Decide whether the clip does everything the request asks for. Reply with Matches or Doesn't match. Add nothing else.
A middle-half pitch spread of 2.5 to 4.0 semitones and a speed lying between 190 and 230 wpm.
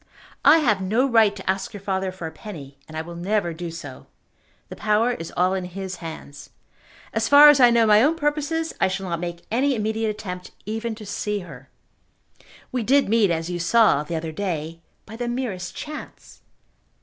Doesn't match